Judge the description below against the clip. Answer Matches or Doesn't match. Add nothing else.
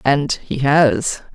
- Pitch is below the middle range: Doesn't match